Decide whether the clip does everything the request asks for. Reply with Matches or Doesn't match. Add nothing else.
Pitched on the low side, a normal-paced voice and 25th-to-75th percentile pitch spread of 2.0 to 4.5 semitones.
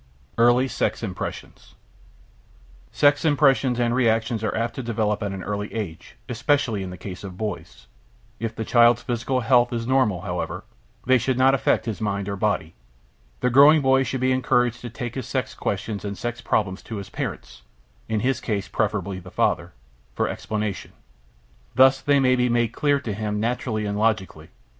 Matches